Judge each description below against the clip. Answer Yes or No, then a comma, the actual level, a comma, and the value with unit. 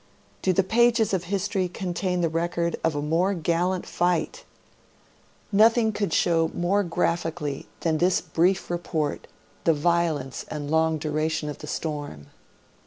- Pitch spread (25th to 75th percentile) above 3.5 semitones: No, average, 3.0 semitones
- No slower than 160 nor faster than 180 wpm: No, average, 140 wpm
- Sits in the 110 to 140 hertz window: No, medium, 170 Hz